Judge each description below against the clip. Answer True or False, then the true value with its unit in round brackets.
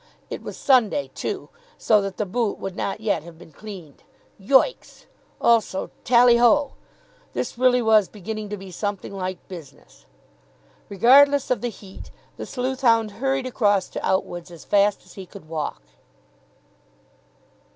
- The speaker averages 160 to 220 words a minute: False (150 wpm)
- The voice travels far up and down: False (4.4 semitones)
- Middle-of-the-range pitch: False (210 Hz)